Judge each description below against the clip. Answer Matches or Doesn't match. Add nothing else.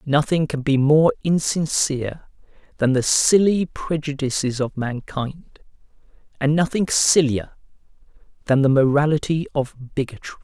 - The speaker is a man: Matches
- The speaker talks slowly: Matches